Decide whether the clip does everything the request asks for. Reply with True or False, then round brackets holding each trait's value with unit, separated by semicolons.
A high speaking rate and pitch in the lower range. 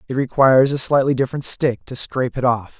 True (215 wpm; 130 Hz)